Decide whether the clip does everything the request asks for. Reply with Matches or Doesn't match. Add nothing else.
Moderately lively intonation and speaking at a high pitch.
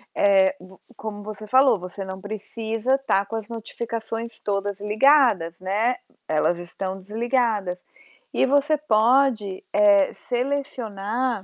Matches